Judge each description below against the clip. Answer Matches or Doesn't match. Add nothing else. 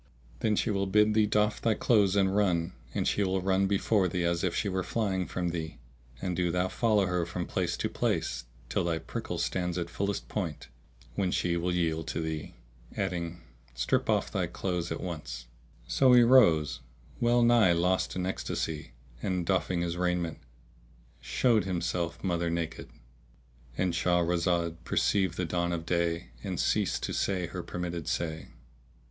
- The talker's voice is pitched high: Doesn't match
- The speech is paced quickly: Doesn't match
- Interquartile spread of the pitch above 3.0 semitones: Doesn't match